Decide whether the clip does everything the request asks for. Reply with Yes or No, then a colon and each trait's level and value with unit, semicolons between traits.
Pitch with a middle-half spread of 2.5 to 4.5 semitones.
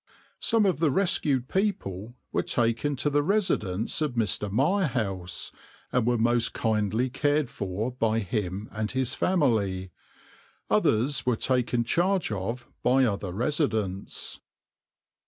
No: wide, 5.5 semitones